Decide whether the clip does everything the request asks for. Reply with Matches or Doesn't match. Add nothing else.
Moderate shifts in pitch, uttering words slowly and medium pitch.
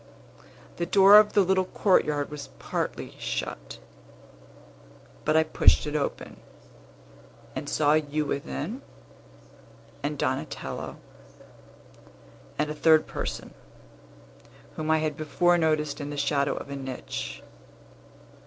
Doesn't match